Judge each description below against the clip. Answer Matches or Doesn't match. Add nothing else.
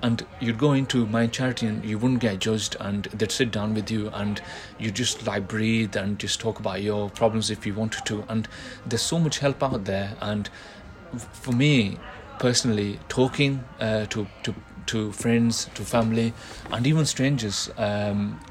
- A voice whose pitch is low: Matches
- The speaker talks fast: Doesn't match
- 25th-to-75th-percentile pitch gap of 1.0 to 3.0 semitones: Matches